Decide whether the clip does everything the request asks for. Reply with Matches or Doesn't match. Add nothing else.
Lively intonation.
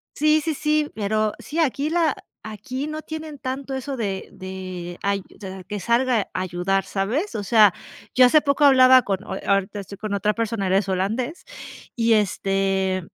Matches